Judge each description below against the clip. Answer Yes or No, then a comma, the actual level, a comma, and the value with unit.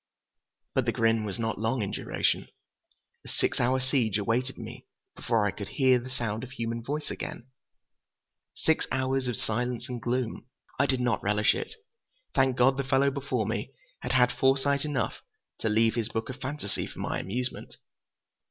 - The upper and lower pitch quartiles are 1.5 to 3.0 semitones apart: Yes, average, 2.7 semitones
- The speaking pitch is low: Yes, low, 125 Hz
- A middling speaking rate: Yes, average, 170 wpm